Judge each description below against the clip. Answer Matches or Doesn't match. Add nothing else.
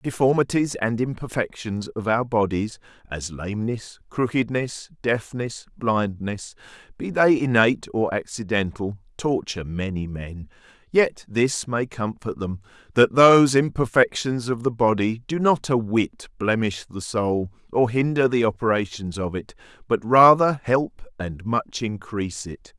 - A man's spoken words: Matches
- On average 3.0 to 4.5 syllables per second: Matches